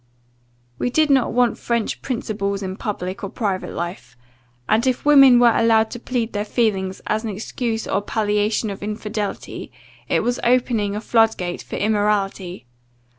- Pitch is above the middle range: Yes, high, 215 Hz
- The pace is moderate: Yes, average, 160 wpm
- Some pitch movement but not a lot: Yes, average, 3.0 semitones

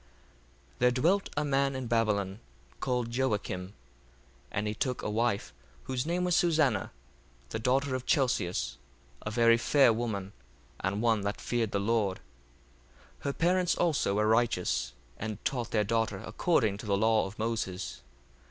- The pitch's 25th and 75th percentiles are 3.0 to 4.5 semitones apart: Yes, average, 4.2 semitones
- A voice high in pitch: No, low, 115 Hz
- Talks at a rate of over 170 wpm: No, average, 160 wpm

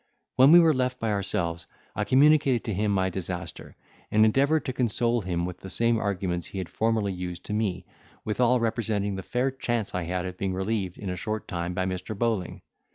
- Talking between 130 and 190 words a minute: No, fast, 205 wpm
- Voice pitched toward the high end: No, low, 105 Hz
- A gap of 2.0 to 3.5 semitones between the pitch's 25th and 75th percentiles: No, average, 4.3 semitones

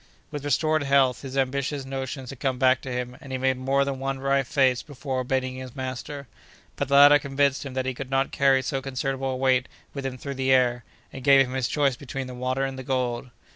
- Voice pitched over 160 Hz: No, low, 135 Hz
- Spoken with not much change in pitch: Yes, narrow, 1.2 semitones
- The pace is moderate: No, fast, 235 wpm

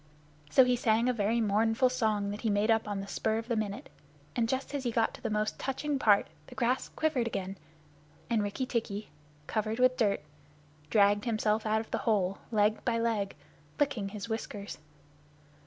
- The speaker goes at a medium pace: Yes, average, 190 wpm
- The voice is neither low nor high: No, high, 220 Hz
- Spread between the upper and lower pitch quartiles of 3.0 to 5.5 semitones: No, narrow, 2.5 semitones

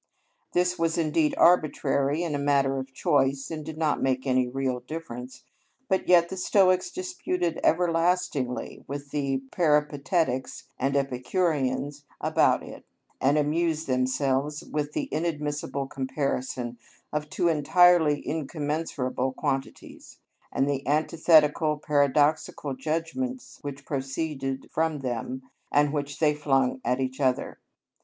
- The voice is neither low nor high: Yes, medium, 145 Hz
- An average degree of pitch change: Yes, average, 3.3 semitones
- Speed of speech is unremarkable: No, slow, 120 wpm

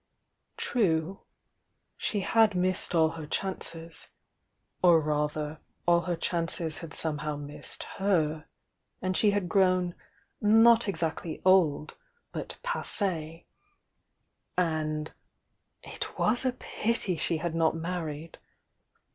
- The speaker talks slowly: Yes, slow, 115 wpm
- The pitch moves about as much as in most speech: Yes, average, 3.3 semitones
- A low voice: No, medium, 170 Hz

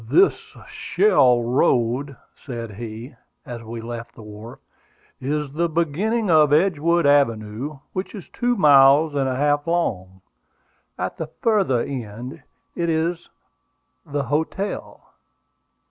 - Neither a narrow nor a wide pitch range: No, wide, 5.9 semitones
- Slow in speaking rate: Yes, slow, 125 wpm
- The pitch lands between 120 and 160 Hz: Yes, medium, 140 Hz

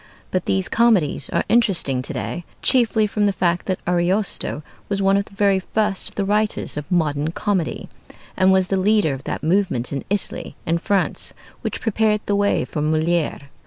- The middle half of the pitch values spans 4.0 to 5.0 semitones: No, average, 3.5 semitones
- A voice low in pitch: No, high, 190 Hz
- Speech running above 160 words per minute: Yes, average, 185 wpm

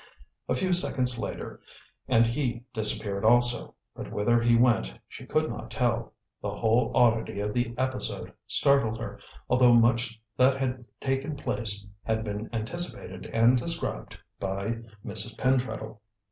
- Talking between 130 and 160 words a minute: Yes, average, 140 wpm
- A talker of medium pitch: No, low, 120 Hz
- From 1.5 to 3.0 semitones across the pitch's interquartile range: Yes, narrow, 2.5 semitones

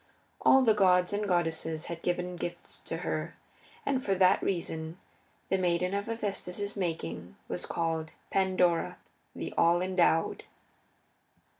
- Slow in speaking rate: Yes, slow, 130 wpm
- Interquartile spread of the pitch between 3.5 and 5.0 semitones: No, average, 2.7 semitones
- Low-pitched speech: No, medium, 180 Hz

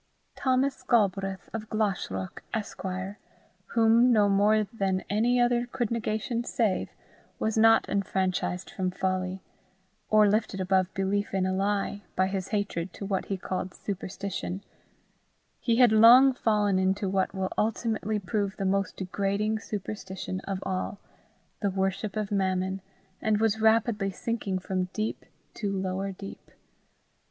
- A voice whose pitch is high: Yes, high, 200 Hz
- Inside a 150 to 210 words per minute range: No, slow, 135 wpm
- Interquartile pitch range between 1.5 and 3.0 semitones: Yes, narrow, 2.5 semitones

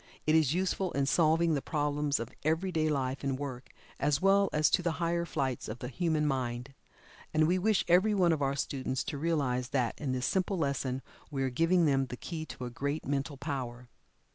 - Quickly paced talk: Yes, fast, 210 wpm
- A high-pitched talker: No, medium, 145 Hz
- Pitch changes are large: No, average, 4.0 semitones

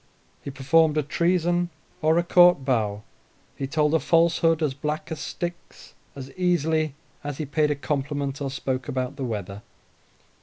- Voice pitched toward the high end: No, medium, 150 Hz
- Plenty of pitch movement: No, average, 3.4 semitones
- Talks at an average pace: Yes, average, 160 wpm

